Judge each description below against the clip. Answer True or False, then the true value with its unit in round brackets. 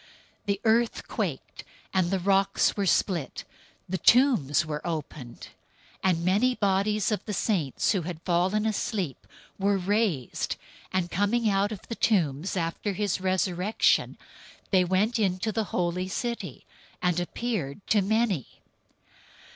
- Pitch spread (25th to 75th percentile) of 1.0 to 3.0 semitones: False (3.4 semitones)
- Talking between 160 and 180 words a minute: False (140 wpm)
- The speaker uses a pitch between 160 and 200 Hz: True (190 Hz)